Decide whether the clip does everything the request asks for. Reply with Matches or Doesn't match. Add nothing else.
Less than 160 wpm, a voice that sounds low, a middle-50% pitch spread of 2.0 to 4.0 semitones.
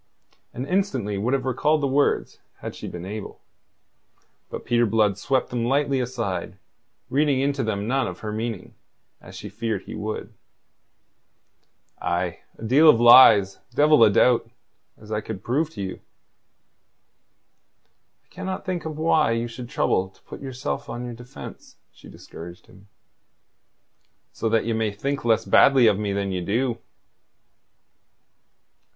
Doesn't match